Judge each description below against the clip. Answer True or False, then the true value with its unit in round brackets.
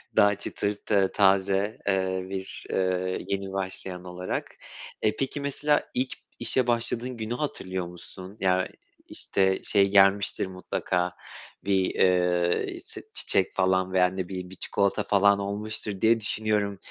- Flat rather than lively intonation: True (1.9 semitones)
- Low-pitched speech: True (95 Hz)